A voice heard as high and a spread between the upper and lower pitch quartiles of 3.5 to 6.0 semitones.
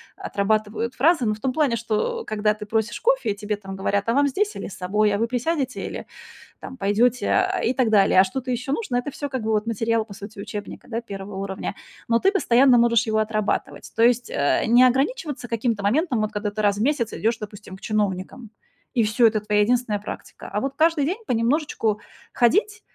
Yes: high, 230 Hz; average, 3.8 semitones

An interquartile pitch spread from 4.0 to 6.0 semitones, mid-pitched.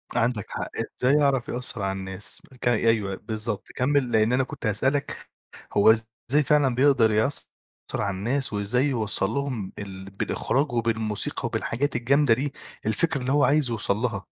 No: average, 4.5 semitones; low, 120 Hz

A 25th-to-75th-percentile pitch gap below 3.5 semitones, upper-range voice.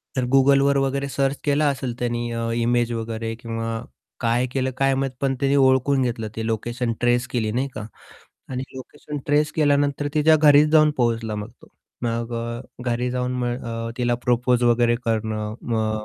No: average, 3.0 semitones; low, 125 Hz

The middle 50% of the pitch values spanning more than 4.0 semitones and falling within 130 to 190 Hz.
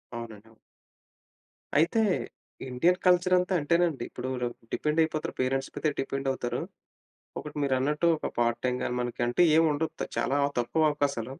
Yes: average, 4.4 semitones; medium, 140 Hz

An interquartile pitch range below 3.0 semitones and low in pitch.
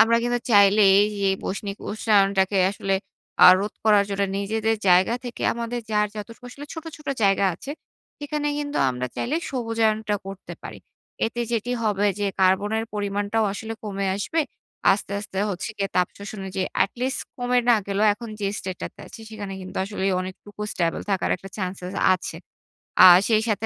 No: narrow, 2.5 semitones; high, 205 Hz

